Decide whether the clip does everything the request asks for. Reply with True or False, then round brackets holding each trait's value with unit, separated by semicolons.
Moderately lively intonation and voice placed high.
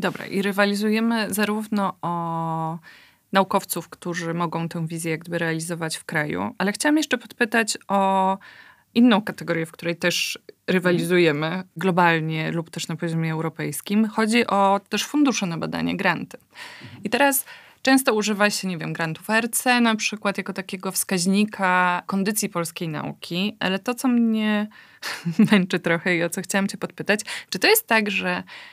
True (4.0 semitones; 195 Hz)